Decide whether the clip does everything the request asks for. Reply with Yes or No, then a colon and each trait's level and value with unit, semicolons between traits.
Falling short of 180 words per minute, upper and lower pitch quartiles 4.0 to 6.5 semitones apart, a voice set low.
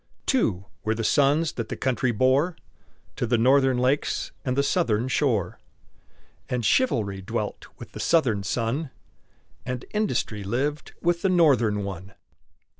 Yes: average, 140 wpm; average, 4.9 semitones; low, 125 Hz